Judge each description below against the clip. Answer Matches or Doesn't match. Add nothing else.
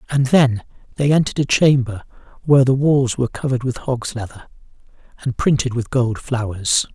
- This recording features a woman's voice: Doesn't match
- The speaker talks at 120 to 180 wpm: Matches